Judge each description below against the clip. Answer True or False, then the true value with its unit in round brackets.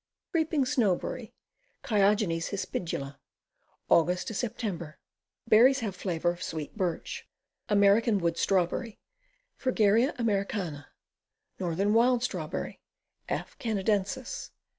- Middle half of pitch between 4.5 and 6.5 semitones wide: True (4.8 semitones)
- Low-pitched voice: False (200 Hz)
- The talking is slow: True (90 wpm)